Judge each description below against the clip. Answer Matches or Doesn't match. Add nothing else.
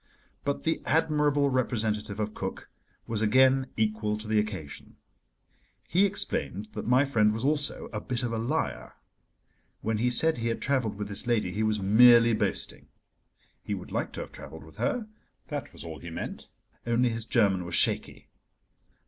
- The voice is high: Doesn't match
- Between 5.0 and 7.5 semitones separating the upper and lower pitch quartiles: Doesn't match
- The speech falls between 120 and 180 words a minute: Matches